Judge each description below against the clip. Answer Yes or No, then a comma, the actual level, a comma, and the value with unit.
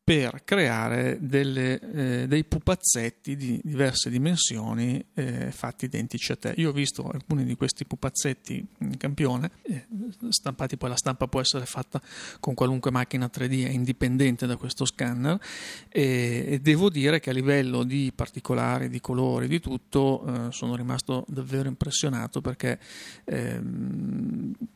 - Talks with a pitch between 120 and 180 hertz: Yes, low, 135 Hz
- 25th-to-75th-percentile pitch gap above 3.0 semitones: No, average, 2.7 semitones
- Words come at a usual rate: Yes, average, 140 wpm